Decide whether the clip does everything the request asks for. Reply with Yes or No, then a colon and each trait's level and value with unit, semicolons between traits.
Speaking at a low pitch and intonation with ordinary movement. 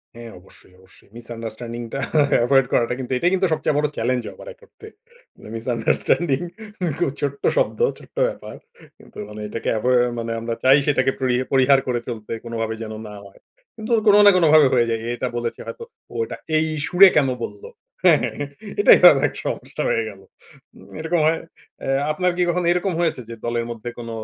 No: low, 130 Hz; wide, 5.8 semitones